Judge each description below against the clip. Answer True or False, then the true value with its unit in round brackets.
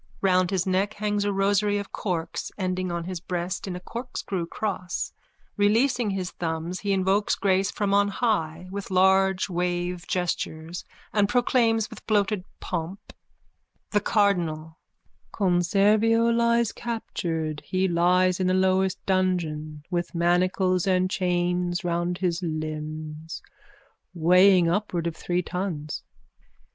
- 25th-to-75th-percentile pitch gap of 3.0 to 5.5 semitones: False (2.6 semitones)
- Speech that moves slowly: True (130 wpm)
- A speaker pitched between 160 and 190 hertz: True (185 Hz)